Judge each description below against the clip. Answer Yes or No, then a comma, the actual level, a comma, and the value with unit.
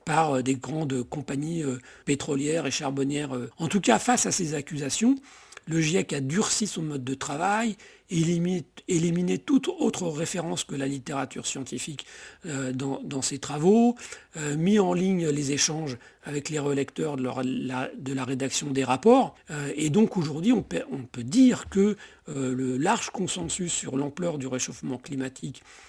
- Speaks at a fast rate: No, average, 155 wpm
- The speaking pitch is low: No, medium, 150 Hz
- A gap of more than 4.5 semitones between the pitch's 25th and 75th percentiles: Yes, average, 5.1 semitones